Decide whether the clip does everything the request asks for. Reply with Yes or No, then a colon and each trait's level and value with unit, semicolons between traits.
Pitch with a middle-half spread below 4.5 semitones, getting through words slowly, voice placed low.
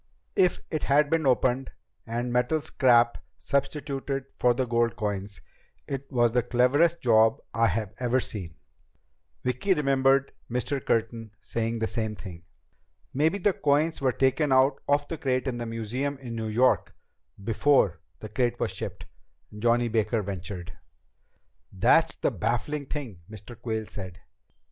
No: average, 3.6 semitones; average, 145 wpm; low, 120 Hz